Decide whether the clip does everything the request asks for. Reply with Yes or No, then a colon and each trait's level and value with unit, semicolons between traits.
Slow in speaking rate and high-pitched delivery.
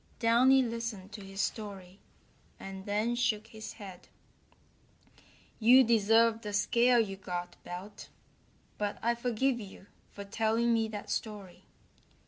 Yes: slow, 125 wpm; high, 220 Hz